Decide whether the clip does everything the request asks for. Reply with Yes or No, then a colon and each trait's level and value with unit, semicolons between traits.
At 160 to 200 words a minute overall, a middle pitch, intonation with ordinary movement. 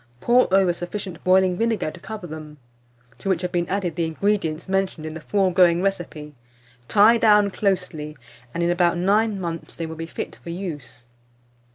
Yes: average, 175 wpm; medium, 180 Hz; average, 3.2 semitones